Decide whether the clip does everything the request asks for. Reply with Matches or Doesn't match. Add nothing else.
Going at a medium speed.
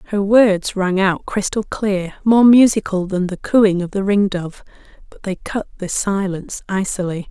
Matches